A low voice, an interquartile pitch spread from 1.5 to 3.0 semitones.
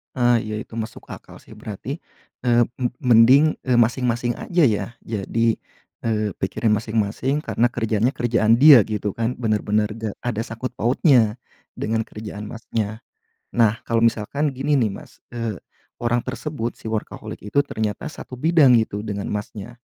Yes: low, 115 Hz; narrow, 2.6 semitones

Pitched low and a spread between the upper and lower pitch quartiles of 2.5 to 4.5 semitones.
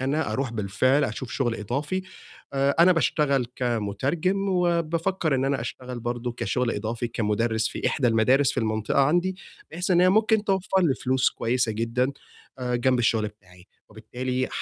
No: low, 130 Hz; wide, 5.4 semitones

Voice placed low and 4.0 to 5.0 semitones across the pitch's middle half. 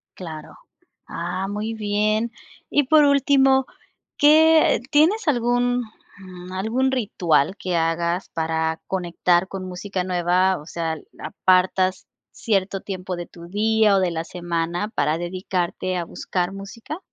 No: high, 190 Hz; average, 4.3 semitones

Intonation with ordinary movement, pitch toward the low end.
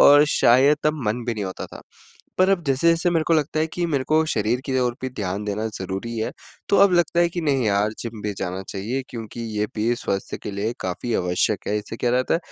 No: wide, 6.4 semitones; low, 120 Hz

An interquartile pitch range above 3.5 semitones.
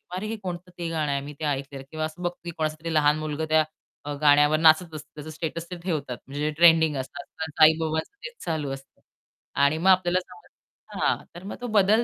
No: average, 2.7 semitones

